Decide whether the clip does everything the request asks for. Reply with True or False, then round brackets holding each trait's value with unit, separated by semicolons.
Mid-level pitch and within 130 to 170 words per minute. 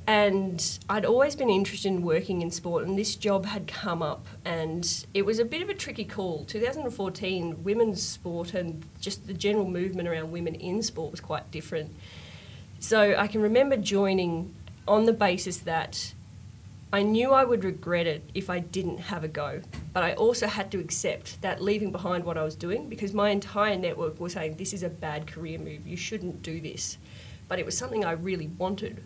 False (180 Hz; 200 wpm)